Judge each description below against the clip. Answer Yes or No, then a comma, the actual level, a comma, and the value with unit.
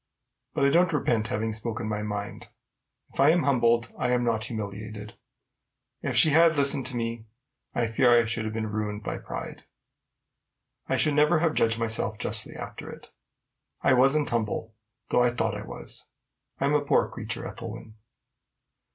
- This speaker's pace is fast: No, average, 170 wpm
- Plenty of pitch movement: No, average, 4.0 semitones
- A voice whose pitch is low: Yes, low, 115 Hz